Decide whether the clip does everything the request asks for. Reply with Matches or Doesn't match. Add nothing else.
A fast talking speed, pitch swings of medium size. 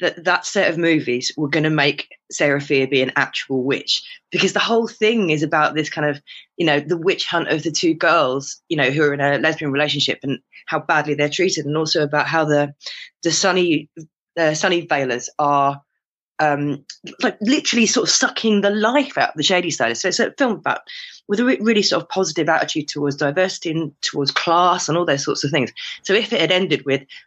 Matches